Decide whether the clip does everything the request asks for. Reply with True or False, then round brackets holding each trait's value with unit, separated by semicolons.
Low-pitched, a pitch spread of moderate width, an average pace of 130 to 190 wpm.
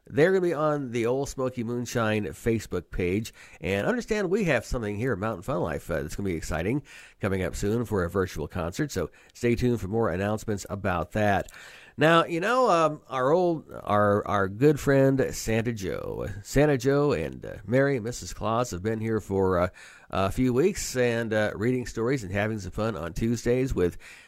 False (110 Hz; 4.8 semitones; 200 wpm)